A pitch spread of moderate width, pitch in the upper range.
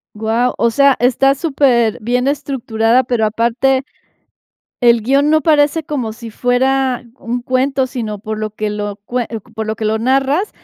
Yes: average, 3.4 semitones; high, 245 Hz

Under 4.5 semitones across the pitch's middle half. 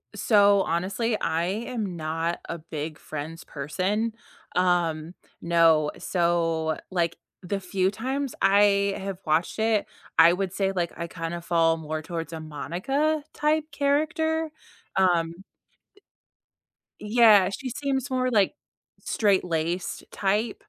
No: average, 4.9 semitones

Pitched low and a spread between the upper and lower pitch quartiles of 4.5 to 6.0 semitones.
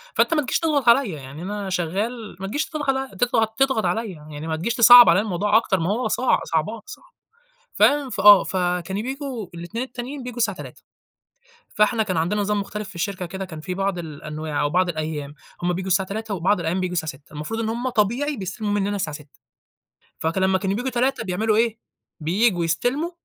No: high, 200 Hz; average, 5.2 semitones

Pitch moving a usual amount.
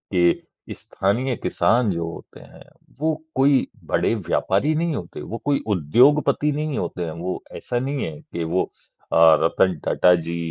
No: wide, 8.5 semitones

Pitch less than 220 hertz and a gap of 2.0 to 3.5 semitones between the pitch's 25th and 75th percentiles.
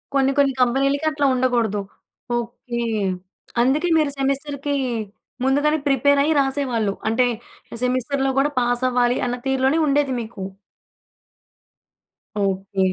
No: very high, 265 Hz; average, 2.7 semitones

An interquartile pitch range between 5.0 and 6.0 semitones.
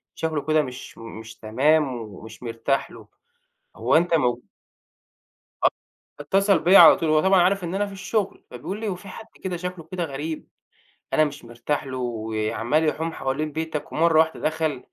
Yes: wide, 5.4 semitones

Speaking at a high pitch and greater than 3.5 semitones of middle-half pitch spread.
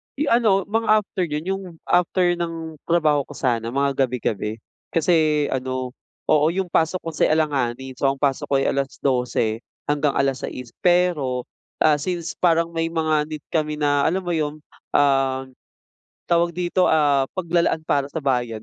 No: medium, 150 Hz; average, 4.0 semitones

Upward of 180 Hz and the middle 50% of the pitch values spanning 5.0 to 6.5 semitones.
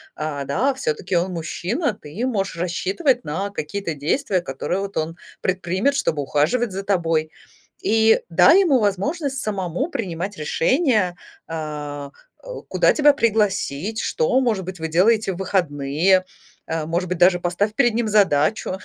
Yes: high, 190 Hz; wide, 5.5 semitones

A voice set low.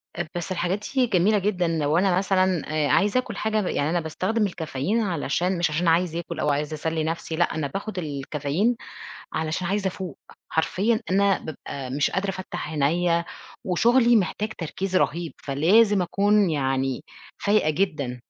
No: medium, 175 Hz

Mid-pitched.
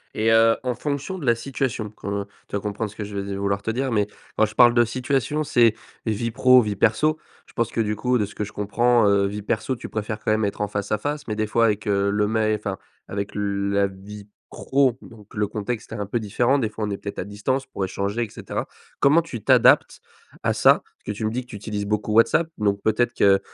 No: low, 110 Hz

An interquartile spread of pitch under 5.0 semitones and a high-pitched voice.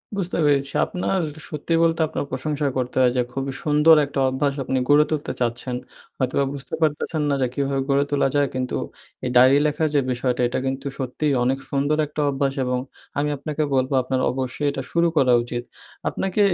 No: narrow, 2.5 semitones; medium, 140 Hz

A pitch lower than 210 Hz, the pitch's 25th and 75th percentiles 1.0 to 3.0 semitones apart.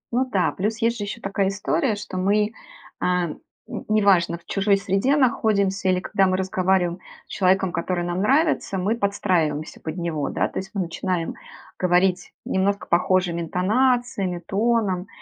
Yes: high, 190 Hz; narrow, 2.5 semitones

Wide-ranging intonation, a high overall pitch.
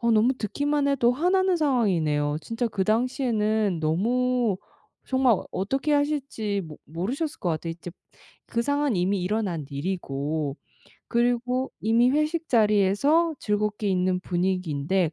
Yes: wide, 6.2 semitones; high, 215 Hz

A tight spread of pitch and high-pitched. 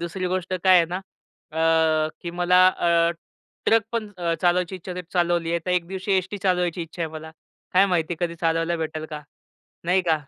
No: narrow, 1.9 semitones; medium, 175 Hz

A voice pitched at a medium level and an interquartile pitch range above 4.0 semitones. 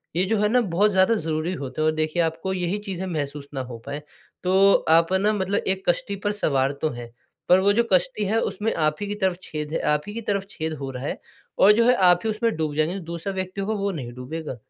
Yes: medium, 180 Hz; average, 4.5 semitones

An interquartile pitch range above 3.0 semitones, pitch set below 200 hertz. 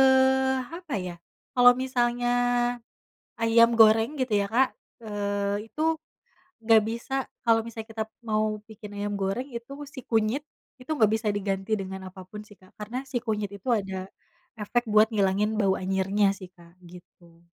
No: average, 3.5 semitones; high, 215 Hz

